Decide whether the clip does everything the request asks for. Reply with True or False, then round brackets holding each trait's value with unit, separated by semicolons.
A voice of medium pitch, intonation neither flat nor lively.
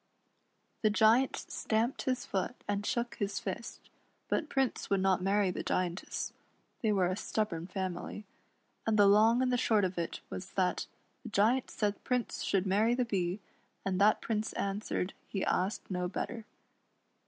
False (205 Hz; 3.3 semitones)